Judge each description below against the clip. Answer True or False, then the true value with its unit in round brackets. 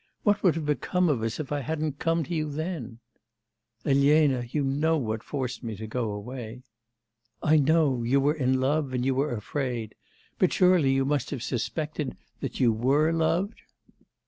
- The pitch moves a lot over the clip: False (3.8 semitones)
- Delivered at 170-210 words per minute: True (175 wpm)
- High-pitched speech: False (140 Hz)